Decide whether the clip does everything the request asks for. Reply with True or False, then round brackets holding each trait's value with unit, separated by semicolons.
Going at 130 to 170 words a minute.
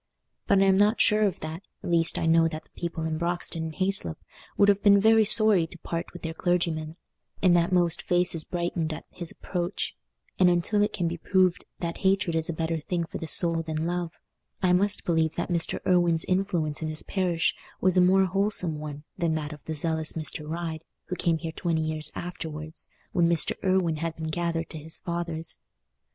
False (205 wpm)